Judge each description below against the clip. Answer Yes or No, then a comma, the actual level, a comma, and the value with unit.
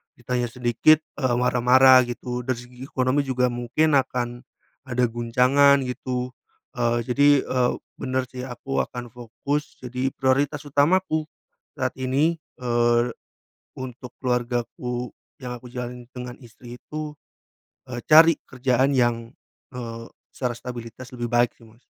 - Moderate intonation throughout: No, narrow, 1.6 semitones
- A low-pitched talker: Yes, low, 125 Hz